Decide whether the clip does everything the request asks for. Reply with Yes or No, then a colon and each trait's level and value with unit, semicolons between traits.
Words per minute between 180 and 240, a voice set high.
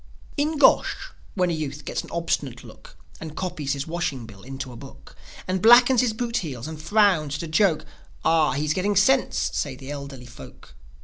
No: average, 190 wpm; medium, 160 Hz